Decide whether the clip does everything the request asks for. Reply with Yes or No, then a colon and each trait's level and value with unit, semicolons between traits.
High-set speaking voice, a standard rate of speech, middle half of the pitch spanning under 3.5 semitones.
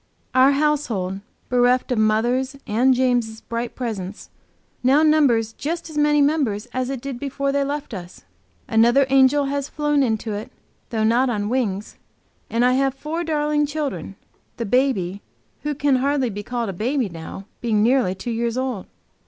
No: very high, 255 Hz; average, 165 wpm; average, 4.1 semitones